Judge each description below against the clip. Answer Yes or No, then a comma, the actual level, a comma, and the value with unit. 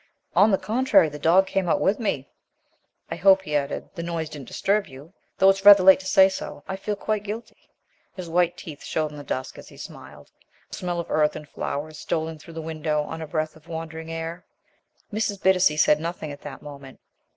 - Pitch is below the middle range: No, medium, 165 Hz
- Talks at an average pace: No, fast, 220 wpm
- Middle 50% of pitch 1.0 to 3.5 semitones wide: No, average, 4.0 semitones